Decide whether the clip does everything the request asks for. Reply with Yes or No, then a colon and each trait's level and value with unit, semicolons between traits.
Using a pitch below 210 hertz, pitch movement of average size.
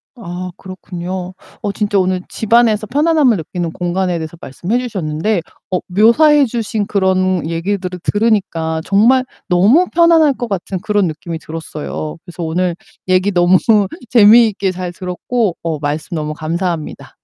Yes: medium, 185 Hz; average, 4.1 semitones